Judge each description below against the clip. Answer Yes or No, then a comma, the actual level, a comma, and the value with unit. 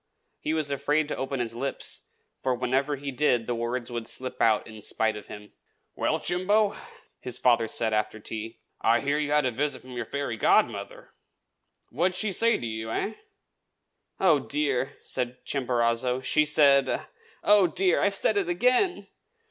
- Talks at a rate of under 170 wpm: No, average, 175 wpm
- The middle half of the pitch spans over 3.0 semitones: Yes, average, 4.5 semitones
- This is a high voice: No, low, 135 Hz